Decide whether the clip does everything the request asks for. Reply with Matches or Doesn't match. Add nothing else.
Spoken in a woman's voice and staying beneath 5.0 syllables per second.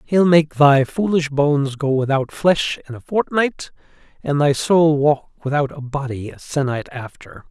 Doesn't match